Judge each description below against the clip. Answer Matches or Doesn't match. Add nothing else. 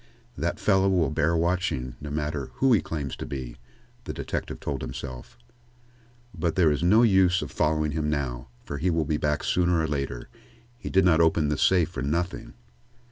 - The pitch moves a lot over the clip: Doesn't match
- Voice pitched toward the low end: Matches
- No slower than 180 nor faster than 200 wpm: Matches